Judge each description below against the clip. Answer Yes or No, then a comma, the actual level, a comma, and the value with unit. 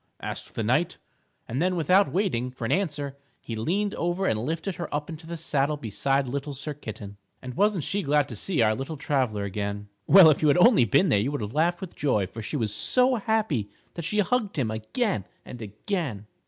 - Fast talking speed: Yes, fast, 215 wpm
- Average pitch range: No, wide, 7.7 semitones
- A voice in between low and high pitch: Yes, medium, 145 Hz